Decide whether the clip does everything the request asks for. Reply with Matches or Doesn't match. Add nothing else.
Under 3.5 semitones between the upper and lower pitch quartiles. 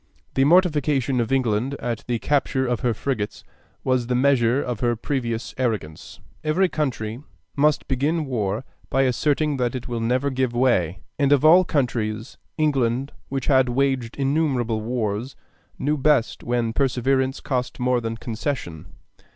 Matches